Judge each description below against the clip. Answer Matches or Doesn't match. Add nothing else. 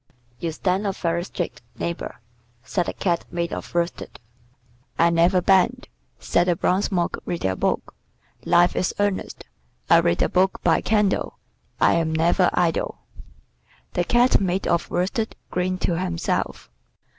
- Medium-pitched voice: Matches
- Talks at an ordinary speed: Matches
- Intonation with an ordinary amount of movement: Doesn't match